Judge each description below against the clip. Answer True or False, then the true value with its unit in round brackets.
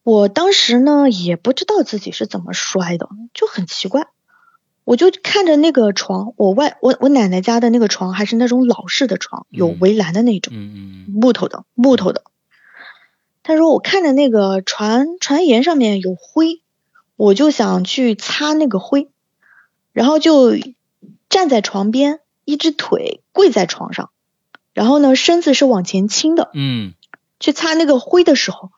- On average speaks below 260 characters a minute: True (230 characters per minute)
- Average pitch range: False (7.4 semitones)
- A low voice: False (240 Hz)